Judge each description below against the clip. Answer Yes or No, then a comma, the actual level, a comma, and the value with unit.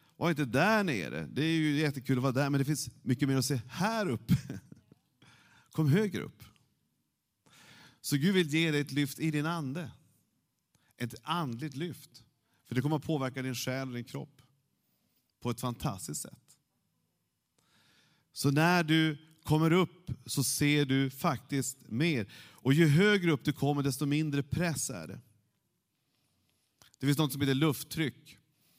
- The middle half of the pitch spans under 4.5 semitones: Yes, average, 3.2 semitones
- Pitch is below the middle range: No, medium, 145 Hz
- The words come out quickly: No, average, 160 wpm